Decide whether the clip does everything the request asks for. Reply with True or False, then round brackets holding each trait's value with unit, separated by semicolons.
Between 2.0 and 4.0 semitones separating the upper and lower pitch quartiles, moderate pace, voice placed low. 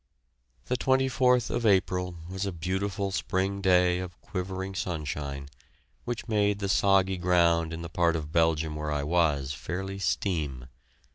True (3.2 semitones; 145 wpm; 90 Hz)